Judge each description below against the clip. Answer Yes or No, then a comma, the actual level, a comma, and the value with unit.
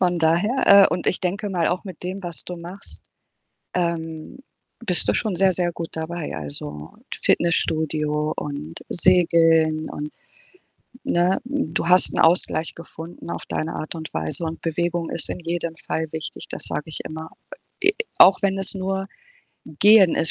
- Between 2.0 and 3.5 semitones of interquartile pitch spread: Yes, narrow, 2.4 semitones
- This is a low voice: No, medium, 170 Hz